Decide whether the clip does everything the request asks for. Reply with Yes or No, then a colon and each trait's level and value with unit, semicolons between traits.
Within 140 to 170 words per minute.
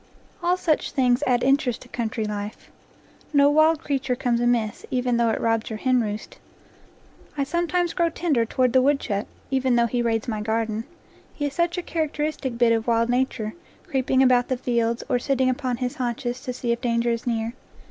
No: average, 190 wpm